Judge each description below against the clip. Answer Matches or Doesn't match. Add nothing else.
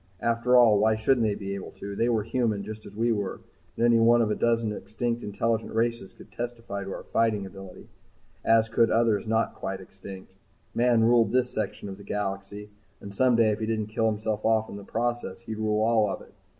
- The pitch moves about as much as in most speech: Doesn't match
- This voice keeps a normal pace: Doesn't match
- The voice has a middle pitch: Doesn't match